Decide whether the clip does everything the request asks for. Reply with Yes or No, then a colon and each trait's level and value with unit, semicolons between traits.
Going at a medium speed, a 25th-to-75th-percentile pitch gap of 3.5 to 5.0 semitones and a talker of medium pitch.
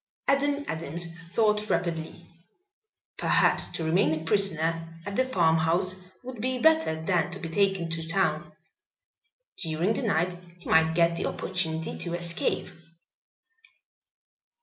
No: slow, 125 wpm; average, 3.8 semitones; medium, 175 Hz